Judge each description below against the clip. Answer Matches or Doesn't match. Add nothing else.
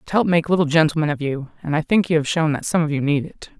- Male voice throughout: Doesn't match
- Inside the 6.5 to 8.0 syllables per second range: Matches